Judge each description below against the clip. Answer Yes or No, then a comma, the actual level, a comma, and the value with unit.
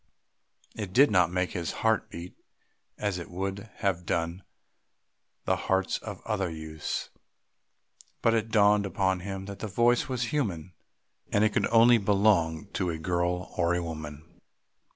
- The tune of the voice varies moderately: Yes, average, 3.5 semitones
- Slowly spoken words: No, average, 155 wpm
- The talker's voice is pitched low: Yes, very low, 95 Hz